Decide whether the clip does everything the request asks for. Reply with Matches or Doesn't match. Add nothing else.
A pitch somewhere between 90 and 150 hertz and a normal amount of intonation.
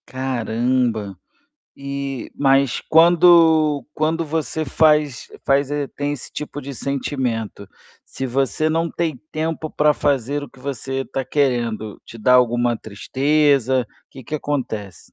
Matches